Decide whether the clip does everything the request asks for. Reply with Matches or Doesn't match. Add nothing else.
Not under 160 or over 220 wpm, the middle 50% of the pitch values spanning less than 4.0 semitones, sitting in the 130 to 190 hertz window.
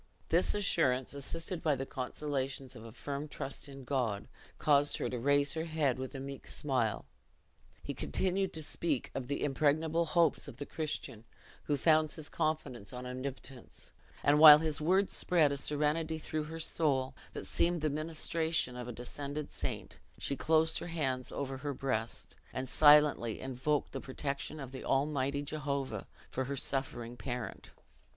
Matches